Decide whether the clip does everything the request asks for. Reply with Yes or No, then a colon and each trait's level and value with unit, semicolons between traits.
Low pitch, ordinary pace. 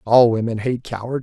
Yes: low, 115 Hz; average, 195 wpm